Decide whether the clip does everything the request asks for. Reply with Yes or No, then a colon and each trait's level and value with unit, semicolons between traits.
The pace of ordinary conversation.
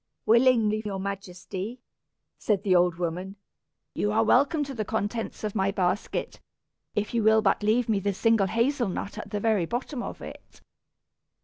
Yes: average, 170 wpm